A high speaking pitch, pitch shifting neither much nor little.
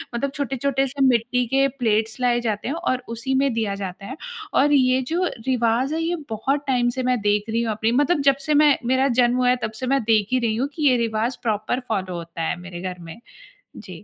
Yes: high, 245 Hz; average, 3.5 semitones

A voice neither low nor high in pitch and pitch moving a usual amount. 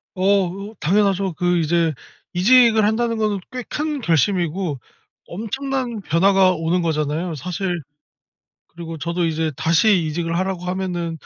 Yes: medium, 180 Hz; average, 3.6 semitones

